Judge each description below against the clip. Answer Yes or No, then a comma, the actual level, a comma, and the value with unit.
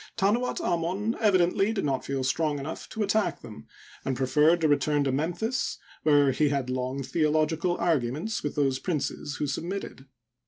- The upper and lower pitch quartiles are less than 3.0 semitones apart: No, average, 4.6 semitones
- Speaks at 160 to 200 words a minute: Yes, average, 165 wpm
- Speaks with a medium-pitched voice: Yes, medium, 155 Hz